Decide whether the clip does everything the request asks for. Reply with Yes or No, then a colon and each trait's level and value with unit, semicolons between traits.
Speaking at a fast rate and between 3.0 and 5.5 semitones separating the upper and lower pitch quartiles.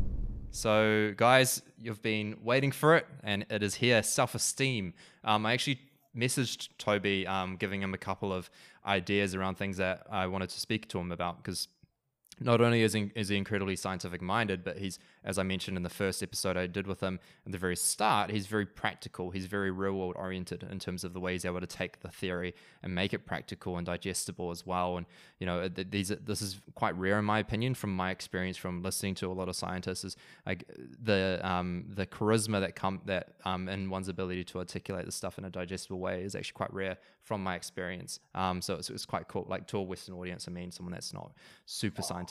No: fast, 220 wpm; narrow, 2.4 semitones